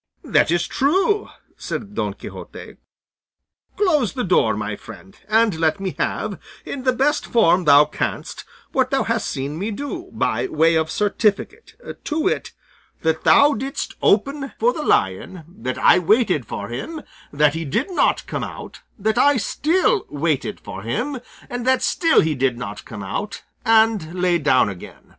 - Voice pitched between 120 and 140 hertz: No, high, 200 Hz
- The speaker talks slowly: No, average, 165 wpm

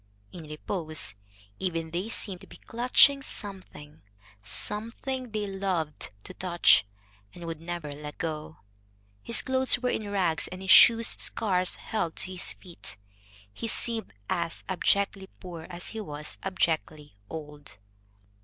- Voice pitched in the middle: Yes, medium, 180 Hz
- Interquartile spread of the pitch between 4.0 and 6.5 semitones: Yes, average, 4.7 semitones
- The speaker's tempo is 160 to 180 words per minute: No, slow, 135 wpm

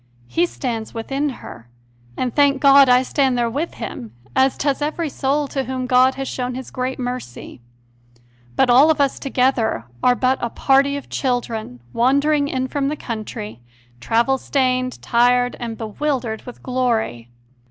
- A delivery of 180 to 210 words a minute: No, average, 160 wpm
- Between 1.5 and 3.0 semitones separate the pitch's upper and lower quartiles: Yes, narrow, 2.5 semitones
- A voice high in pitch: Yes, very high, 255 Hz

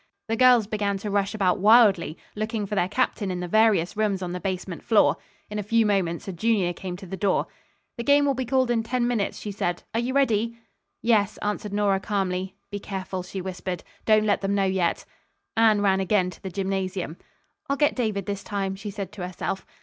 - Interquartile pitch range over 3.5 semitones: No, narrow, 2.6 semitones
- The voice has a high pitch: Yes, high, 200 Hz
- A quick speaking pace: Yes, fast, 210 wpm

